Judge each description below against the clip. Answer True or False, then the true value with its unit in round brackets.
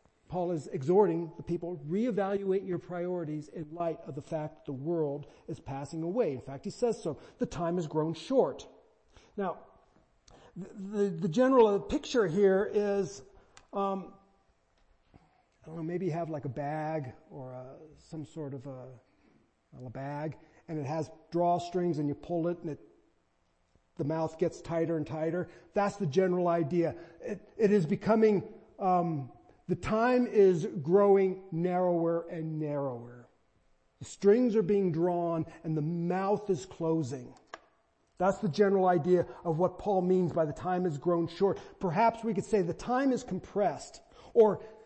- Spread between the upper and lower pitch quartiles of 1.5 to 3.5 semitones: False (4.0 semitones)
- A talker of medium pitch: True (170 Hz)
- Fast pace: False (160 wpm)